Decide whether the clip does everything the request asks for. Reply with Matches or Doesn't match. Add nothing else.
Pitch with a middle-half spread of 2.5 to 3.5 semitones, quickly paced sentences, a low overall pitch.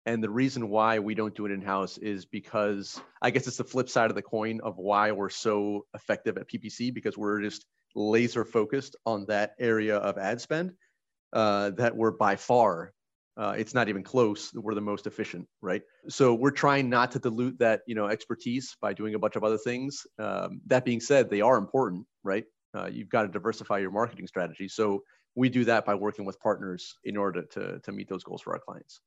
Matches